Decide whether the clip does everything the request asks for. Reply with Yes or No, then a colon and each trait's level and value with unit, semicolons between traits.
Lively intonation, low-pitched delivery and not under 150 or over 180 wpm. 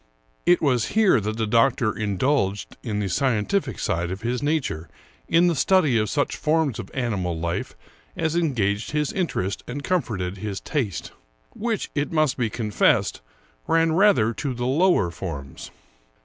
Yes: wide, 7.3 semitones; low, 125 Hz; average, 155 wpm